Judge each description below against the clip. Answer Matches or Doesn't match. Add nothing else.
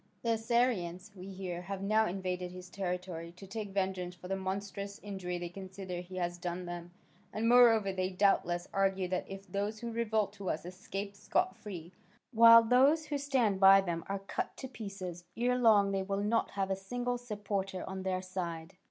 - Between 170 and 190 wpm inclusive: Matches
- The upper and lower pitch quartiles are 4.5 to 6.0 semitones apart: Doesn't match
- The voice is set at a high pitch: Matches